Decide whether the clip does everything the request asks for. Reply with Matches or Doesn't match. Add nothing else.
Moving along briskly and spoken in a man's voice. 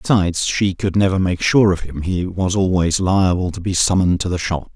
Matches